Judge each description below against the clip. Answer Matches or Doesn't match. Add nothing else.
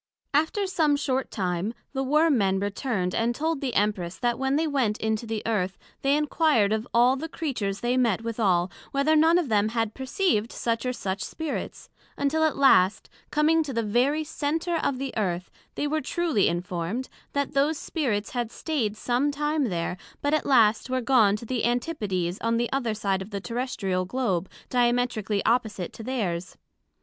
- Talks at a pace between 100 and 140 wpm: Doesn't match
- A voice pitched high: Matches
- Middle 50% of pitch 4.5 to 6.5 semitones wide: Matches